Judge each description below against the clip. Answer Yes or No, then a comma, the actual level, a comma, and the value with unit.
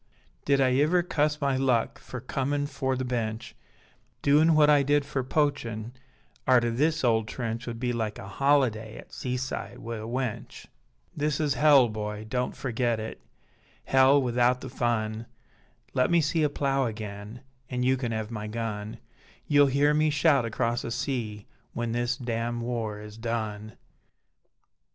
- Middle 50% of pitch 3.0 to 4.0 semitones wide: Yes, average, 3.6 semitones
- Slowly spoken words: No, average, 160 wpm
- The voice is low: Yes, low, 125 Hz